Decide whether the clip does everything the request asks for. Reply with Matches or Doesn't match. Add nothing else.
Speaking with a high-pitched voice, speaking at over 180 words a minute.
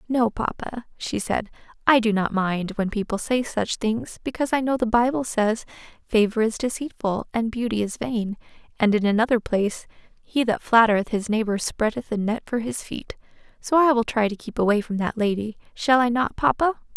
Matches